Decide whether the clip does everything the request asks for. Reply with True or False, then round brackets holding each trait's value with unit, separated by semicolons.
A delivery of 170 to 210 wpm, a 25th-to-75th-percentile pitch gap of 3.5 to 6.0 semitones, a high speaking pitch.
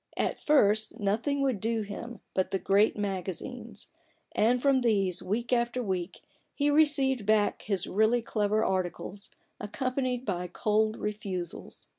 False (135 wpm; 3.8 semitones; 215 Hz)